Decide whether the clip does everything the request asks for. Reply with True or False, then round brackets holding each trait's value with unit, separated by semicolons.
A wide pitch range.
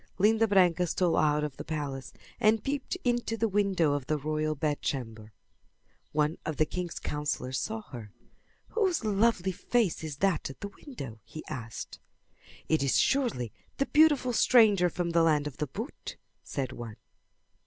True (7.2 semitones)